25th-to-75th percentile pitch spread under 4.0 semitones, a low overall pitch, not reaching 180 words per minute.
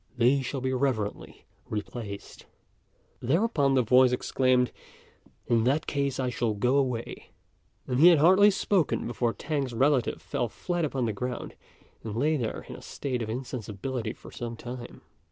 Yes: average, 3.0 semitones; low, 125 Hz; average, 155 wpm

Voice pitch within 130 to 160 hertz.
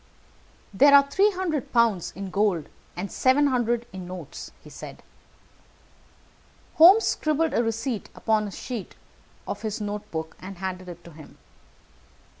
No: high, 220 Hz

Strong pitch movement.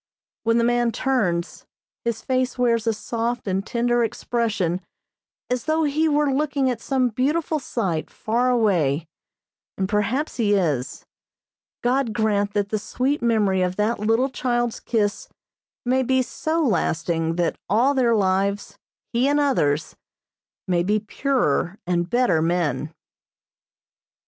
No: average, 5.0 semitones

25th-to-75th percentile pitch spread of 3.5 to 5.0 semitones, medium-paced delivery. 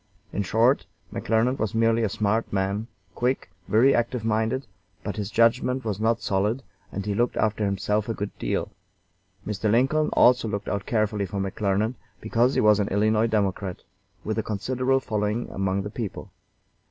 No: narrow, 2.4 semitones; average, 165 wpm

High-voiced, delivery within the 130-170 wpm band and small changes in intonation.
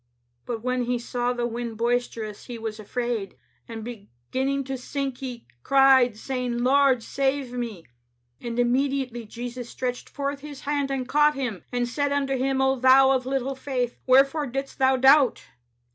Yes: very high, 255 Hz; average, 160 wpm; narrow, 2.1 semitones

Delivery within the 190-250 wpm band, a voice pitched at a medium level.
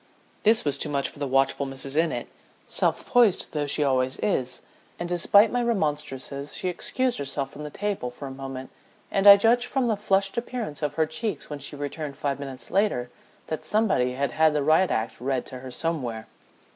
Yes: average, 195 wpm; medium, 150 Hz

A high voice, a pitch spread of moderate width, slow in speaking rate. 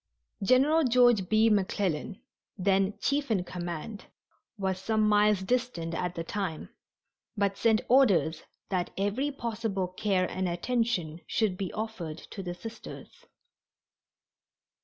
Yes: high, 200 Hz; average, 3.8 semitones; slow, 120 wpm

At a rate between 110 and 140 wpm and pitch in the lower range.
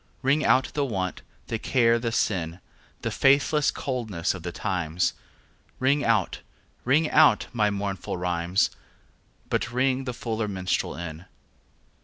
Yes: slow, 135 wpm; low, 110 Hz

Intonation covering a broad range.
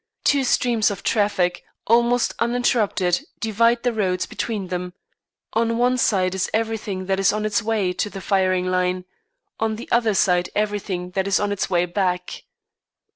No: average, 3.7 semitones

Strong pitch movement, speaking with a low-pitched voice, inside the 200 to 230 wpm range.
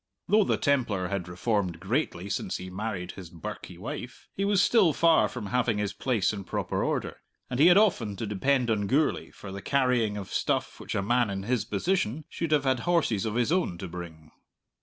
Yes: wide, 6.4 semitones; low, 110 Hz; fast, 205 wpm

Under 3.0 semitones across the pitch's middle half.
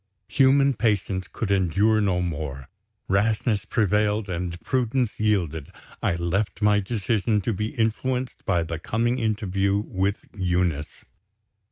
No: average, 3.7 semitones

